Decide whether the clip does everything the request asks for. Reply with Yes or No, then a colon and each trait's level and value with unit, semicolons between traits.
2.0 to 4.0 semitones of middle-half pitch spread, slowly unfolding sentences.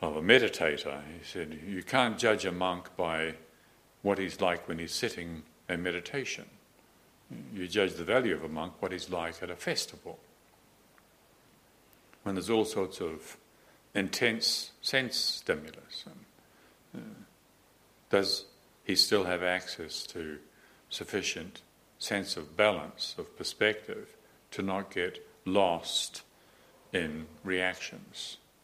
Yes: average, 2.8 semitones; slow, 125 wpm